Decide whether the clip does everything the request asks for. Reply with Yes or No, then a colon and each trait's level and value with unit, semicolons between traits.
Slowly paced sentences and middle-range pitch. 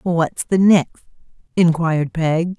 Yes: slow, 115 wpm; medium, 170 Hz